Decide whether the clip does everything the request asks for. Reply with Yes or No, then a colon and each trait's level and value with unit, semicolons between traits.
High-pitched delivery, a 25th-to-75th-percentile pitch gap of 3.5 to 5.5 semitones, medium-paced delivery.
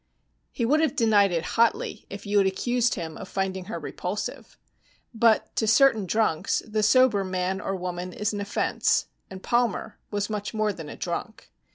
No: high, 205 Hz; average, 3.1 semitones; average, 180 wpm